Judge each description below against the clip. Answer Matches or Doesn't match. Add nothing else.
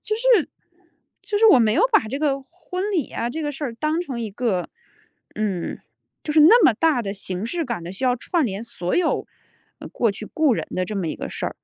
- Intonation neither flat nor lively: Doesn't match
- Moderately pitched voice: Doesn't match